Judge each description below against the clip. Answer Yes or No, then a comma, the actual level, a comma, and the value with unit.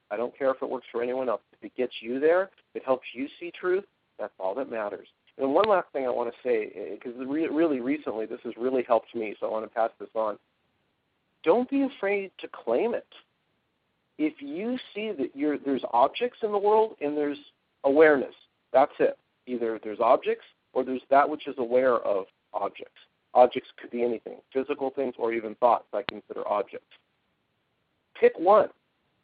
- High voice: No, medium, 140 Hz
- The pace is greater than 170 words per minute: Yes, average, 190 wpm